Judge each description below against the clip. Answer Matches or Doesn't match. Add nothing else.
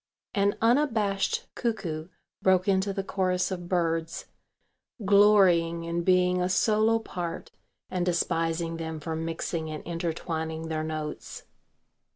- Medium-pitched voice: Matches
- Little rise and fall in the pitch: Doesn't match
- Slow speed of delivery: Matches